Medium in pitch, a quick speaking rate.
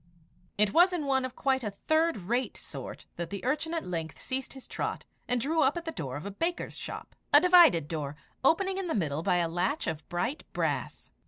No: very high, 255 Hz; fast, 220 wpm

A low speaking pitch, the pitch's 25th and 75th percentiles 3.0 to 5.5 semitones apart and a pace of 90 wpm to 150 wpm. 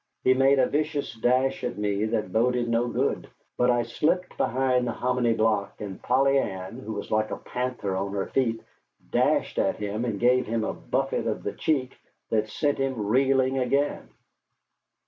No: low, 125 Hz; average, 3.5 semitones; average, 180 wpm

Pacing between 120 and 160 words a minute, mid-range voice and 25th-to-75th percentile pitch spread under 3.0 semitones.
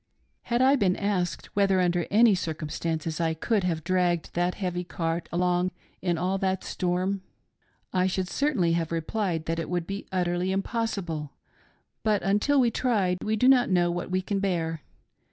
No: average, 170 wpm; medium, 180 Hz; narrow, 2.6 semitones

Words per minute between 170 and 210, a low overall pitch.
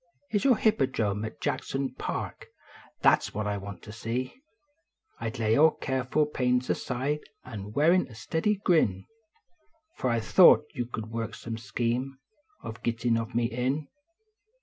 No: average, 160 wpm; low, 120 Hz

